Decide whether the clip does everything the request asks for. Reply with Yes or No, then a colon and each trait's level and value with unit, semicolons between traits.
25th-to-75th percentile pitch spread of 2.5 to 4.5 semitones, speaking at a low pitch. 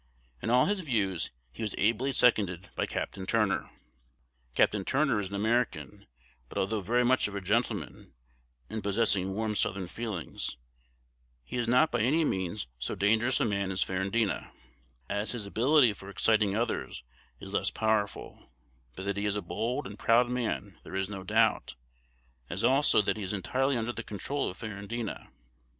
Yes: average, 3.4 semitones; low, 110 Hz